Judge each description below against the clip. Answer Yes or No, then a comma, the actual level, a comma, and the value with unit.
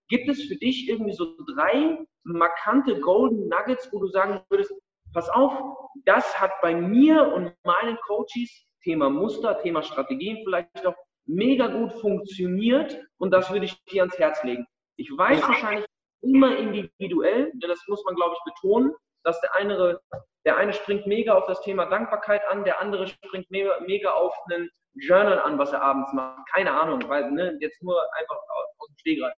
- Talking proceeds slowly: No, average, 175 wpm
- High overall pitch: Yes, high, 205 Hz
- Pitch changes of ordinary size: No, wide, 6.7 semitones